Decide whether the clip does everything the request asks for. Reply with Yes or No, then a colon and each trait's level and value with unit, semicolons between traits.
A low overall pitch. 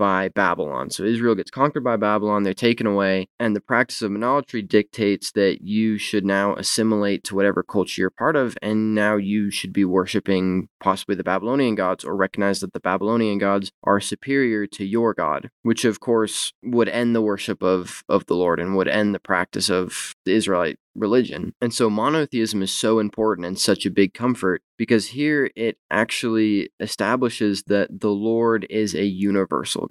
Yes: low, 105 Hz